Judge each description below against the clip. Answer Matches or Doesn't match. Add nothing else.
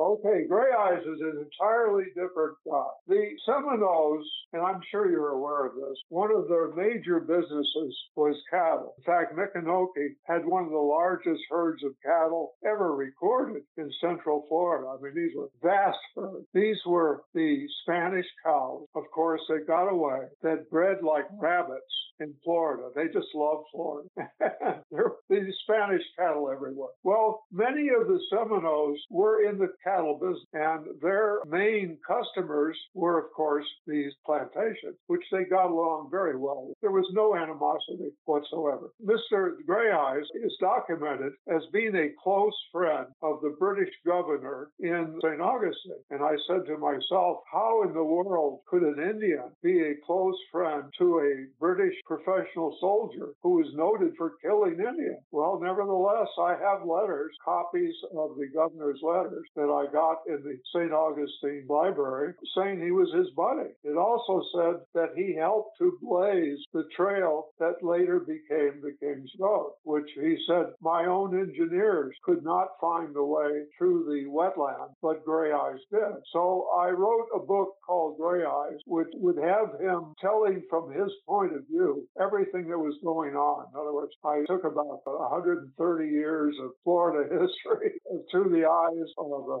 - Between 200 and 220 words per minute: Doesn't match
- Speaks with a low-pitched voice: Doesn't match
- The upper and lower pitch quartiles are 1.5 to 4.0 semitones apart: Doesn't match